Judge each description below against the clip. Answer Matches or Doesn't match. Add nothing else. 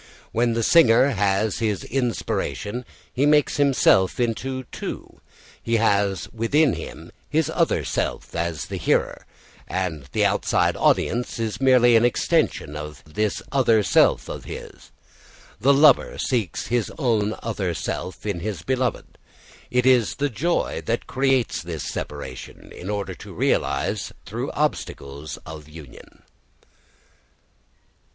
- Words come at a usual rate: Doesn't match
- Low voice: Matches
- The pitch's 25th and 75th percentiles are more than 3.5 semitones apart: Matches